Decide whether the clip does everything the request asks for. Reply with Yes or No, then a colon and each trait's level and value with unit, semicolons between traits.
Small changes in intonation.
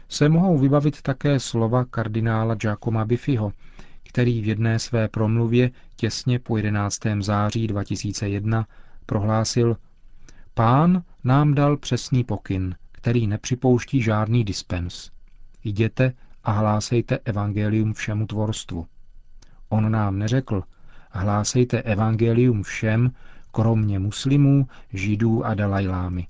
No: average, 3.1 semitones